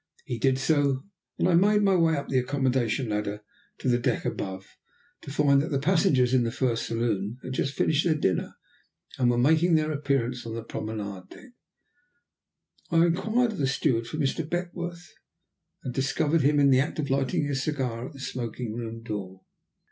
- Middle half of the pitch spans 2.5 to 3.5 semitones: No, average, 4.7 semitones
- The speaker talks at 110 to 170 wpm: No, average, 185 wpm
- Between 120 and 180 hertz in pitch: Yes, low, 135 Hz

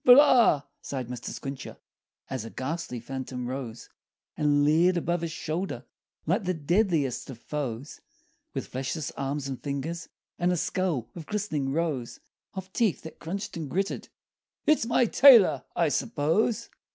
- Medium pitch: Yes, medium, 155 Hz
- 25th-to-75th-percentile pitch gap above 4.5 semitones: Yes, wide, 5.6 semitones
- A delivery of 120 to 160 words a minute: Yes, average, 150 wpm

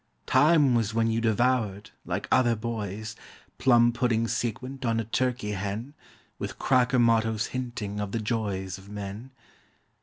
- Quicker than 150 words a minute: No, average, 145 wpm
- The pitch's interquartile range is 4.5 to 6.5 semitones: No, average, 3.0 semitones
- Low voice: Yes, low, 115 Hz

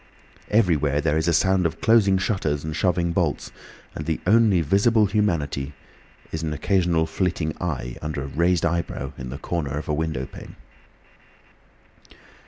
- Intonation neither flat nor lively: Yes, average, 3.9 semitones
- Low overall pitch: Yes, very low, 85 Hz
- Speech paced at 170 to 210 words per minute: No, average, 155 wpm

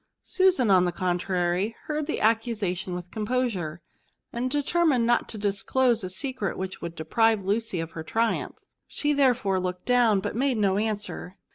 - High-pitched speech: Yes, high, 215 Hz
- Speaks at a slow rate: No, average, 165 wpm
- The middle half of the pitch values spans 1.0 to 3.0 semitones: No, average, 5.1 semitones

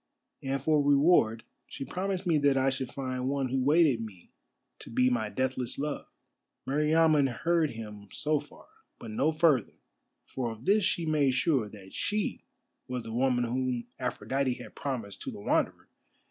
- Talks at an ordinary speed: Yes, average, 165 wpm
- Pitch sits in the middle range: No, low, 130 Hz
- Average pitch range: Yes, average, 3.9 semitones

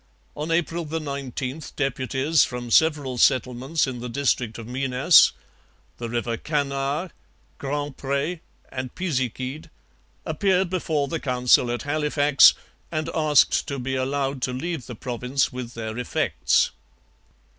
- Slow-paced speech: Yes, slow, 125 wpm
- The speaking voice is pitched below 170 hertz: Yes, low, 135 Hz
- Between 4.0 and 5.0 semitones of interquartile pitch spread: No, average, 3.3 semitones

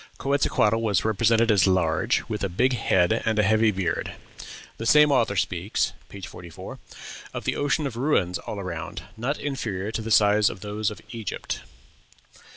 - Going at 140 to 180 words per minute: Yes, average, 160 wpm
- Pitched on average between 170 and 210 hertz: No, low, 105 Hz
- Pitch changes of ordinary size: Yes, average, 3.5 semitones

